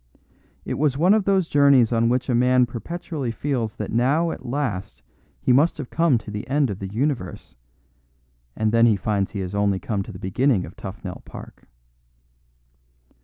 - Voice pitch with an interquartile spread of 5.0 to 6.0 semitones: Yes, wide, 5.4 semitones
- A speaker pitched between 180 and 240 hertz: No, low, 120 Hz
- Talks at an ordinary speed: Yes, average, 175 wpm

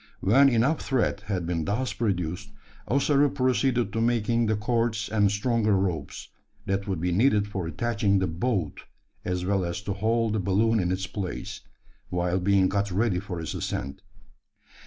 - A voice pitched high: No, low, 100 Hz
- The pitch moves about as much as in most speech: Yes, average, 3.9 semitones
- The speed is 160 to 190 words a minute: Yes, average, 165 wpm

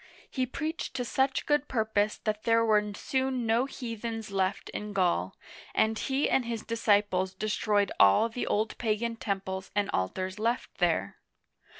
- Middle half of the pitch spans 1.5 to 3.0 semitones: Yes, average, 2.7 semitones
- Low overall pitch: No, high, 220 Hz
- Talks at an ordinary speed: Yes, average, 155 wpm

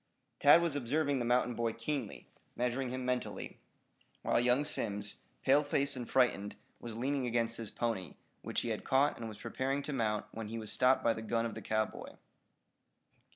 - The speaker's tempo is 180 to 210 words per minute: Yes, average, 185 wpm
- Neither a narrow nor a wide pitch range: Yes, average, 3.1 semitones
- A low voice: Yes, low, 120 Hz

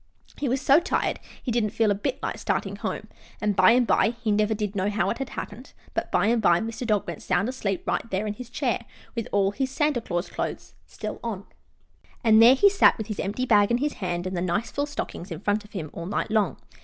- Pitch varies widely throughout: No, average, 3.4 semitones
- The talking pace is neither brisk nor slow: No, fast, 240 wpm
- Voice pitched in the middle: No, high, 215 Hz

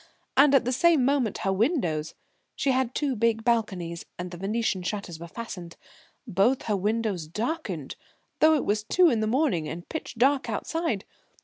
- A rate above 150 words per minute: Yes, average, 175 wpm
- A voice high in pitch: Yes, high, 225 Hz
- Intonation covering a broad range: Yes, wide, 6.1 semitones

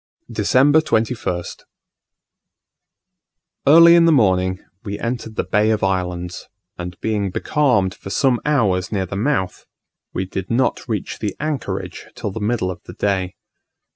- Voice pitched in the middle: No, low, 105 Hz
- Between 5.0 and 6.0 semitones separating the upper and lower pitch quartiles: Yes, average, 5.3 semitones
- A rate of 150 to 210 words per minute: No, average, 140 wpm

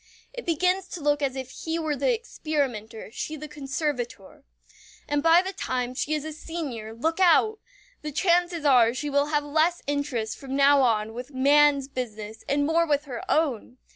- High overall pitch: Yes, very high, 290 Hz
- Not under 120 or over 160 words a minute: No, average, 180 wpm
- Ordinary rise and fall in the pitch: Yes, average, 4.0 semitones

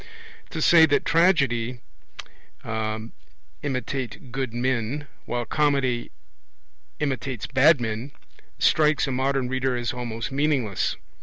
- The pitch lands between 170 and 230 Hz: No, low, 130 Hz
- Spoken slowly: Yes, slow, 100 wpm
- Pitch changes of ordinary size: Yes, average, 3.0 semitones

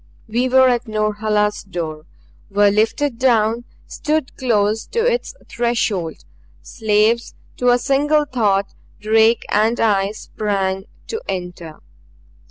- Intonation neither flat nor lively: Yes, average, 3.2 semitones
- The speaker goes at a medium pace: No, slow, 115 wpm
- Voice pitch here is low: No, high, 220 Hz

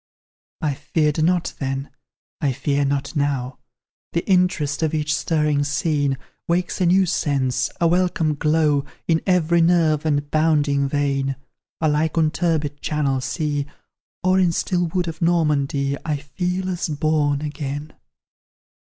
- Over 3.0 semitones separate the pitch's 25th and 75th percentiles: No, average, 2.7 semitones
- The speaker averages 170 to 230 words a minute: No, slow, 135 wpm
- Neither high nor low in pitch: Yes, medium, 150 Hz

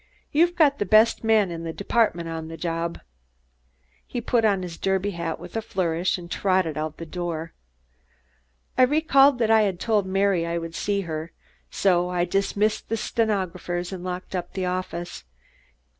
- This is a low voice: No, medium, 185 Hz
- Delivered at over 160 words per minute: Yes, average, 175 wpm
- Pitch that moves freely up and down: No, average, 4.1 semitones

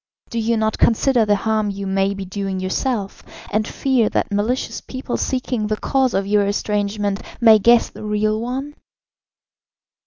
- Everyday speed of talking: Yes, average, 160 wpm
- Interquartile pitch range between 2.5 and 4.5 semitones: Yes, average, 2.8 semitones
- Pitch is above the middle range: Yes, high, 215 Hz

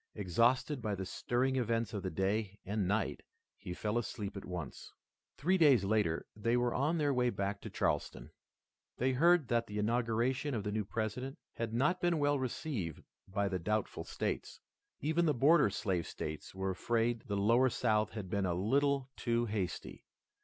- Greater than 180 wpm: No, average, 175 wpm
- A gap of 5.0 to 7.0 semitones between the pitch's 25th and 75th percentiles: No, average, 4.6 semitones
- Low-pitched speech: Yes, low, 115 Hz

